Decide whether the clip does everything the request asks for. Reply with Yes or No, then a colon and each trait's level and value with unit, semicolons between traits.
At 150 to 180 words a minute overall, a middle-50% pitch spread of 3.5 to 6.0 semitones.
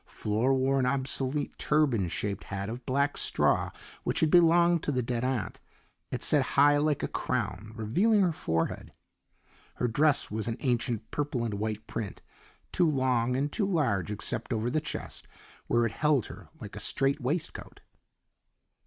Yes: average, 165 wpm; average, 4.6 semitones